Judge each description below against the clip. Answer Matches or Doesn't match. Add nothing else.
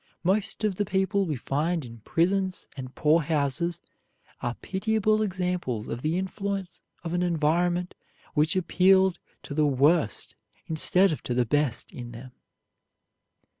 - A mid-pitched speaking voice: Matches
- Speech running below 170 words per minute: Matches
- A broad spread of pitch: Doesn't match